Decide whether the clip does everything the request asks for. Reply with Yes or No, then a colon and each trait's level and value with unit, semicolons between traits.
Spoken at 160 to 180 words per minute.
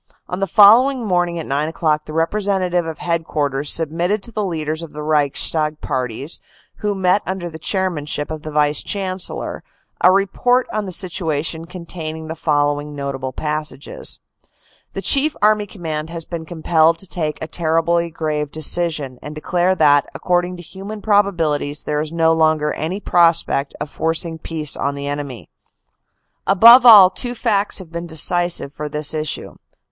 Yes: average, 165 wpm